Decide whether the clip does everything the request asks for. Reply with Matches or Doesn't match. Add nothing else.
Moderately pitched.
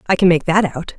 Matches